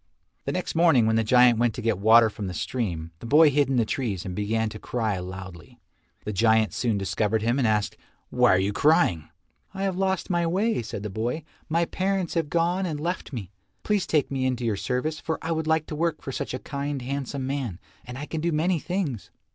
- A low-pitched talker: Yes, low, 130 Hz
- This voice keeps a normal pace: No, fast, 225 wpm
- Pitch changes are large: Yes, wide, 6.7 semitones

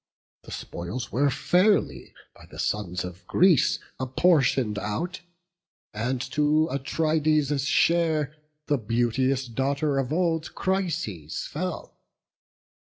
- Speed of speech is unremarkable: No, slow, 100 wpm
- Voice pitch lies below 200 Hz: Yes, medium, 140 Hz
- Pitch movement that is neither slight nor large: Yes, average, 4.8 semitones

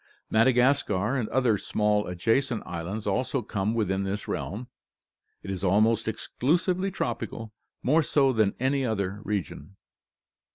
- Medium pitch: No, low, 110 Hz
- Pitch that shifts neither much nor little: Yes, average, 4.7 semitones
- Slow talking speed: Yes, slow, 125 wpm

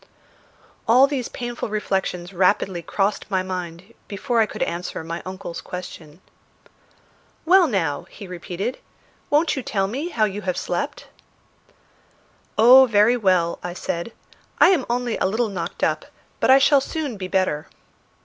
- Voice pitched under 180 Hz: No, high, 200 Hz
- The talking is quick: No, average, 150 wpm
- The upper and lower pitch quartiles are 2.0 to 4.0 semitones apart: No, average, 5.2 semitones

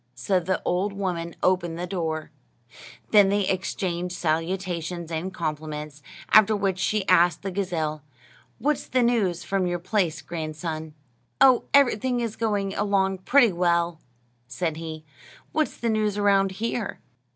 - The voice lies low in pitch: No, medium, 185 Hz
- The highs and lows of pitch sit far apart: No, average, 3.5 semitones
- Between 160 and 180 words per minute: No, average, 140 wpm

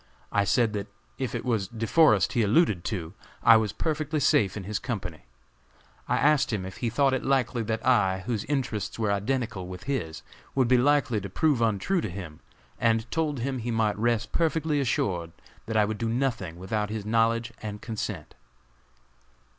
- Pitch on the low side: Yes, low, 115 Hz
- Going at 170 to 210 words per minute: Yes, average, 185 wpm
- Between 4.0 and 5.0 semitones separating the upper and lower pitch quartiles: Yes, average, 4.3 semitones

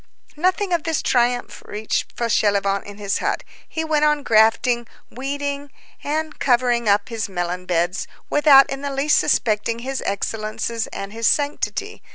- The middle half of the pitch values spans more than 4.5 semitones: Yes, average, 5.3 semitones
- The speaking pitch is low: No, high, 240 Hz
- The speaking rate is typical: Yes, average, 150 wpm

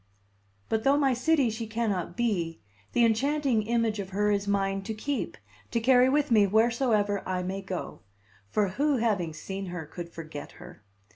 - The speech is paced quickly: No, average, 170 wpm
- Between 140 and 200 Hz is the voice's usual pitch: No, high, 215 Hz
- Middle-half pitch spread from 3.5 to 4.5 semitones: Yes, average, 3.9 semitones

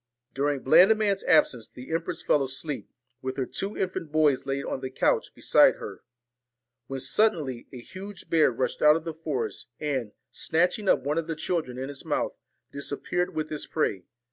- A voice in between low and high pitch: Yes, medium, 150 Hz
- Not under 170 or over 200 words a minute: Yes, average, 175 wpm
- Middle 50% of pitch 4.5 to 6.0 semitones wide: No, average, 4.0 semitones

